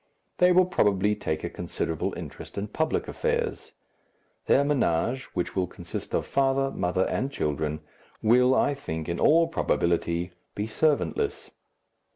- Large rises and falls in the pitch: Yes, wide, 9.0 semitones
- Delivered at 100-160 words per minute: Yes, average, 140 wpm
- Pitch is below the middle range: Yes, low, 120 Hz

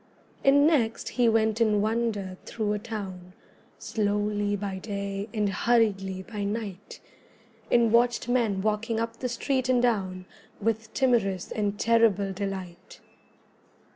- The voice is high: Yes, high, 215 Hz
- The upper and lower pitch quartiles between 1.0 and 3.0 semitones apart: Yes, average, 2.7 semitones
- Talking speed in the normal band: No, slow, 130 wpm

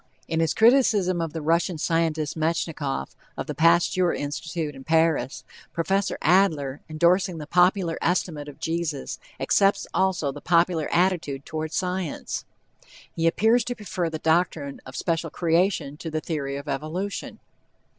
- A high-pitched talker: No, medium, 165 Hz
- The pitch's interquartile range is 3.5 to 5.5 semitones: No, average, 2.8 semitones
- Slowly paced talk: No, average, 145 wpm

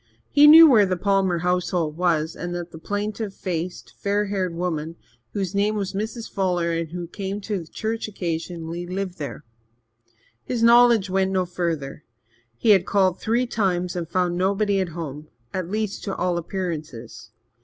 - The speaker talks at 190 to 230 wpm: No, average, 165 wpm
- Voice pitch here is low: No, medium, 185 Hz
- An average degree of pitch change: Yes, average, 3.1 semitones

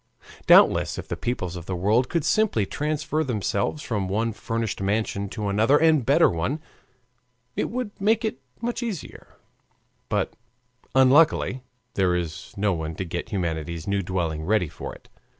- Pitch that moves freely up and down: Yes, wide, 8.3 semitones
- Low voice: Yes, low, 105 Hz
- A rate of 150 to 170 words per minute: Yes, average, 155 wpm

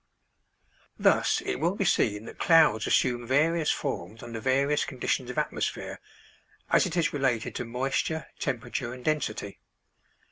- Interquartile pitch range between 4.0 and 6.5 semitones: Yes, average, 4.5 semitones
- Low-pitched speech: Yes, low, 130 Hz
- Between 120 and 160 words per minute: Yes, average, 140 wpm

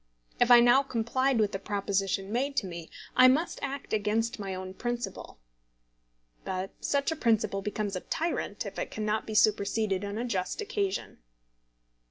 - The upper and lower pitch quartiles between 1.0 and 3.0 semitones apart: No, average, 4.3 semitones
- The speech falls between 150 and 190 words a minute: Yes, average, 165 wpm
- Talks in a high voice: Yes, high, 220 Hz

